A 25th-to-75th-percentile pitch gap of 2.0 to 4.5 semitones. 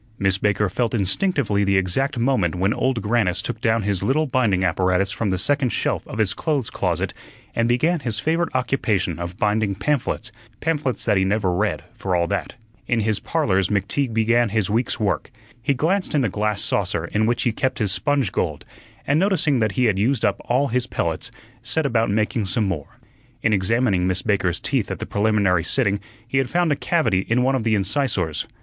No: average, 4.9 semitones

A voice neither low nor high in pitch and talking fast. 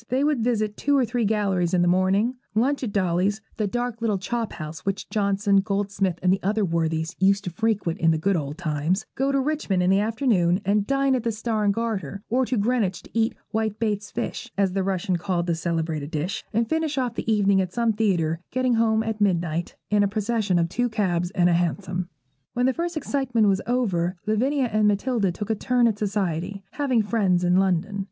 No: high, 205 Hz; fast, 215 wpm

